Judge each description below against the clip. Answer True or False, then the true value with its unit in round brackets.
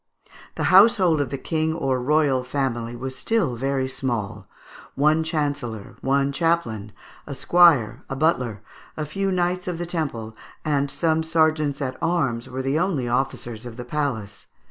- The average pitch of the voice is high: False (140 Hz)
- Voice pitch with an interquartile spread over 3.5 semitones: True (4.5 semitones)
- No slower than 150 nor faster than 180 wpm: True (155 wpm)